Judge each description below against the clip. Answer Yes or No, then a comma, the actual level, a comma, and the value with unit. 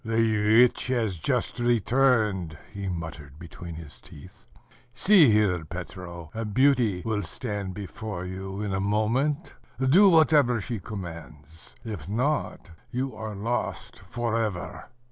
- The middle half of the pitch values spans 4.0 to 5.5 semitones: Yes, average, 5.1 semitones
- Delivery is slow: Yes, slow, 130 wpm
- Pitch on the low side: Yes, low, 105 Hz